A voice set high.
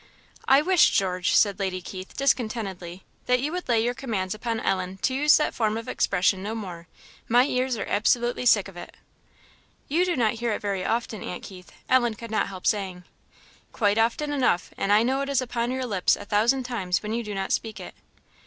Yes: high, 220 Hz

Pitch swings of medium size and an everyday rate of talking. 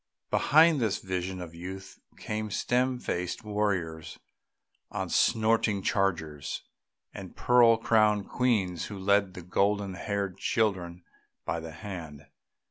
No: average, 3.4 semitones; slow, 115 wpm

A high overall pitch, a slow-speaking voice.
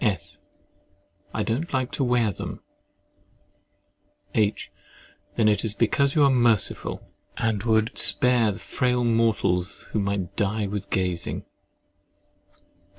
No: low, 110 Hz; slow, 120 wpm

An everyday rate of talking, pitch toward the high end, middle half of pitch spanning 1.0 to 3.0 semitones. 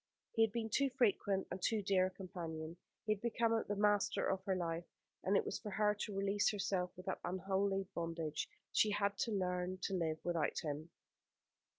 Yes: average, 195 wpm; high, 195 Hz; narrow, 2.6 semitones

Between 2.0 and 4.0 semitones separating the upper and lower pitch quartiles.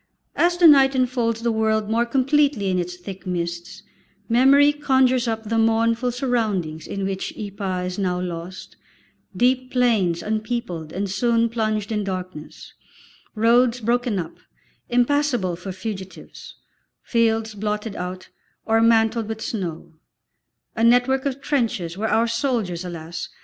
No: average, 4.6 semitones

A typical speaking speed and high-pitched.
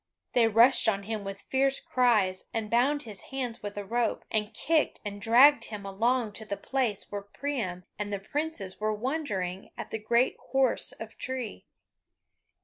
Yes: average, 170 wpm; high, 225 Hz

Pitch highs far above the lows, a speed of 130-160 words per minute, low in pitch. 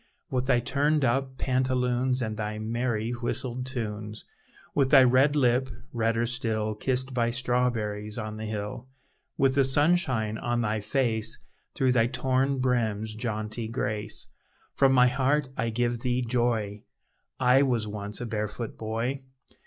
No: average, 2.9 semitones; average, 145 wpm; low, 120 Hz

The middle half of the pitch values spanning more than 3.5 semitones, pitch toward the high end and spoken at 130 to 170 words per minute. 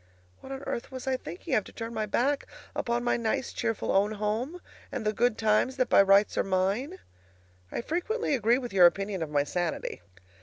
No: average, 4.6 semitones; high, 225 Hz; average, 200 wpm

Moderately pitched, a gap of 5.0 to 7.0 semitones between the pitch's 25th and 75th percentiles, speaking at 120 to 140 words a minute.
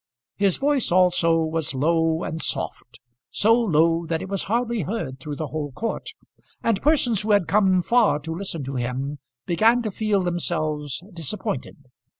No: medium, 170 Hz; wide, 5.4 semitones; average, 160 wpm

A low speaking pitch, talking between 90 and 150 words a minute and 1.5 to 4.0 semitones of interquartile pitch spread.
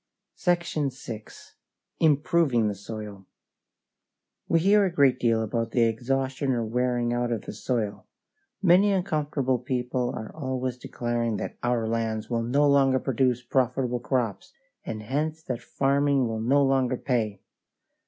Yes: low, 125 Hz; average, 140 wpm; average, 3.3 semitones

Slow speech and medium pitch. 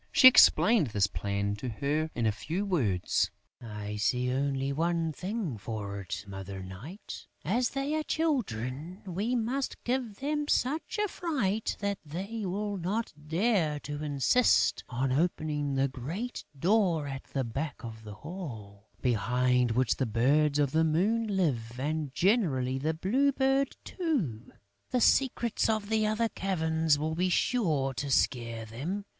No: average, 150 wpm; medium, 155 Hz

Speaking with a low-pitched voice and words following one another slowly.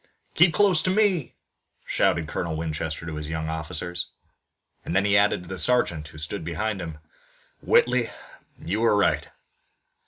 No: very low, 85 Hz; average, 155 wpm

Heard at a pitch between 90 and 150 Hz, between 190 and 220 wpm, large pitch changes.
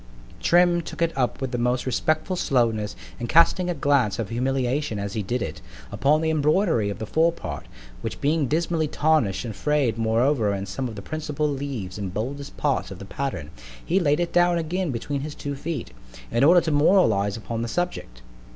Yes: medium, 140 Hz; average, 195 wpm; wide, 5.8 semitones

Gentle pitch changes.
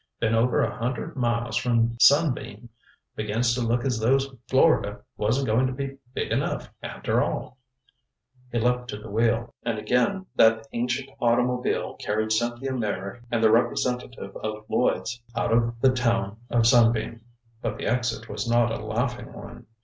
Yes: narrow, 1.7 semitones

